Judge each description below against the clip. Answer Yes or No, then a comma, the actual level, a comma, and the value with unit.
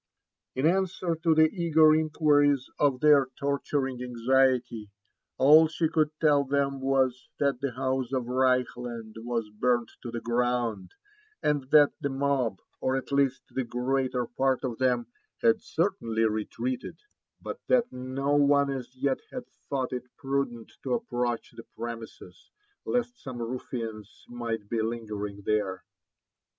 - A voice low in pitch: Yes, low, 130 Hz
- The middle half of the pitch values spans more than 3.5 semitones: No, average, 3.2 semitones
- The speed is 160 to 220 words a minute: No, average, 140 wpm